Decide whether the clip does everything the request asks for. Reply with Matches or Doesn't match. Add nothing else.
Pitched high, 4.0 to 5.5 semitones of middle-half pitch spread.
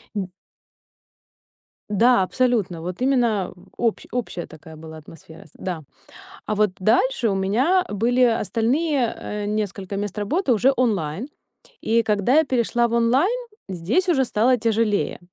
Matches